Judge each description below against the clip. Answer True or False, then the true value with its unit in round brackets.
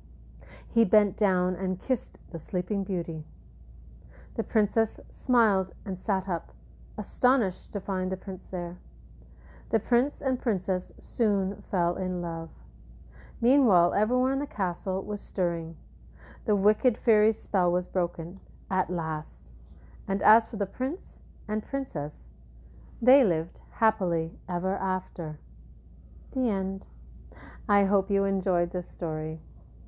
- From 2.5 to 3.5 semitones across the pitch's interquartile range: False (4.6 semitones)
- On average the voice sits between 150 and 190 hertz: True (185 Hz)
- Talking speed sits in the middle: False (125 wpm)